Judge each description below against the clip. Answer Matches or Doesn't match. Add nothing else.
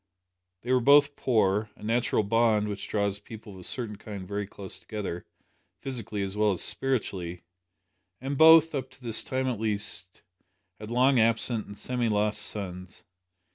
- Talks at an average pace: Matches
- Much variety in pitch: Doesn't match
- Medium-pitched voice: Doesn't match